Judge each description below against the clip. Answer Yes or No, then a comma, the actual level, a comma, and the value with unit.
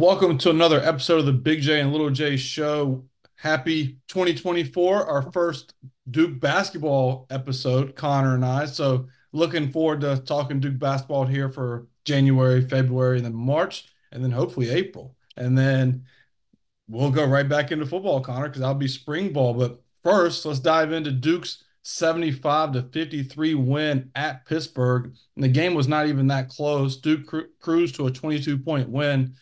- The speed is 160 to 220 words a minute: Yes, average, 170 wpm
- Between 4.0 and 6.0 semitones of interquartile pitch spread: No, average, 3.1 semitones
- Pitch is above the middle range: No, medium, 140 Hz